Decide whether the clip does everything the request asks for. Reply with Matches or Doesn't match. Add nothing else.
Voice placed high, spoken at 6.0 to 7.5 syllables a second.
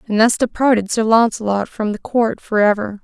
Doesn't match